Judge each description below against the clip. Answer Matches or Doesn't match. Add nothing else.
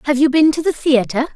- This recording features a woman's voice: Matches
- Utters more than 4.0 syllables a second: Matches